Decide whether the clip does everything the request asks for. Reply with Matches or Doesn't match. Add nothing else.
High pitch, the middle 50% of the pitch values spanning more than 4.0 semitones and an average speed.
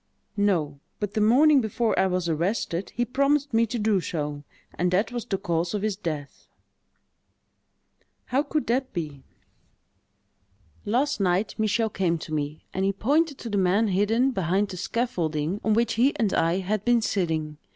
Matches